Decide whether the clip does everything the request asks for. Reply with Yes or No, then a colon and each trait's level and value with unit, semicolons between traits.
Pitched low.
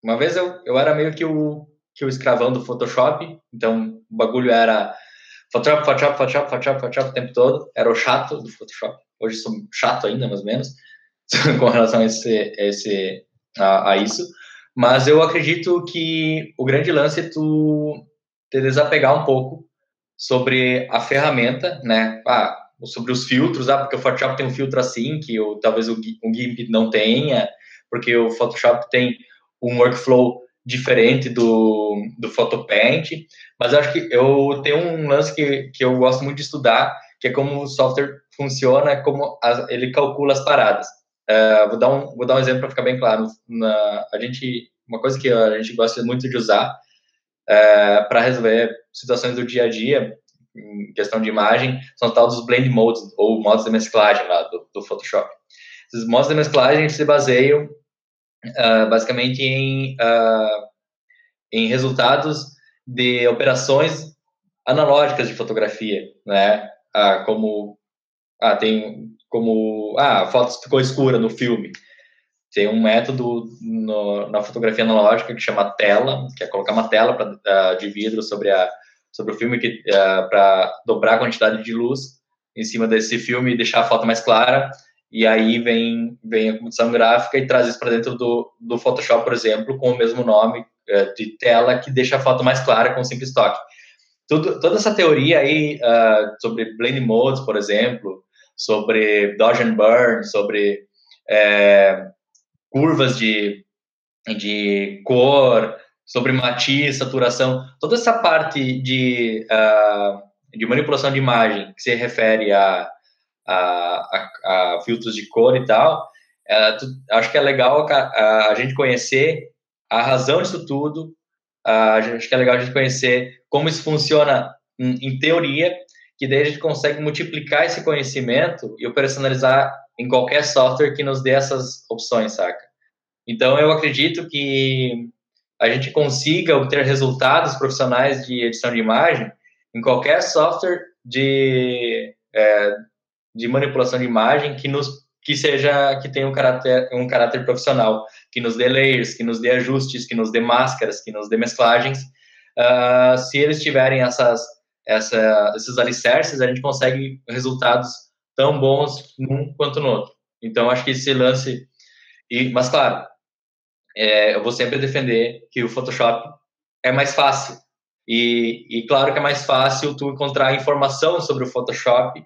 Yes: low, 125 Hz